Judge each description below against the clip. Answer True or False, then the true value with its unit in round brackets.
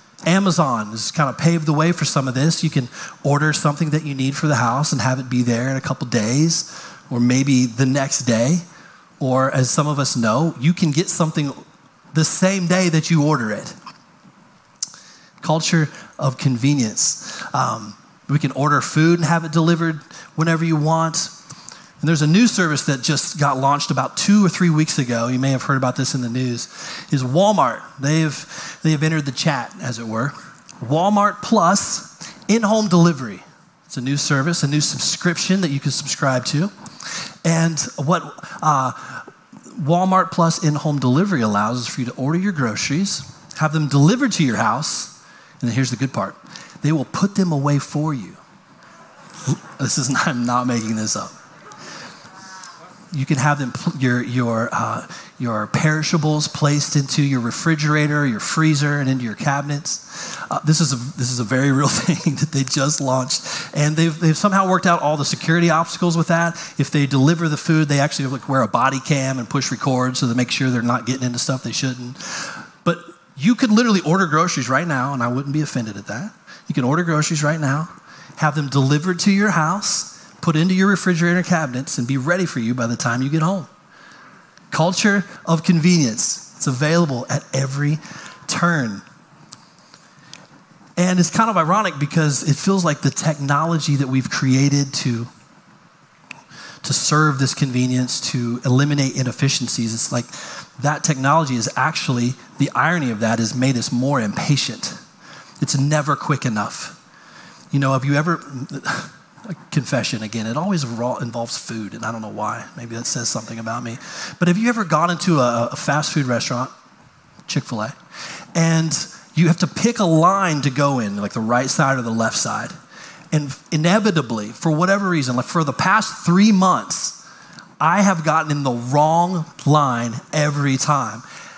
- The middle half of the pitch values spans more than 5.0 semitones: False (4.3 semitones)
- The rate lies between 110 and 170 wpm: False (180 wpm)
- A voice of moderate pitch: True (150 Hz)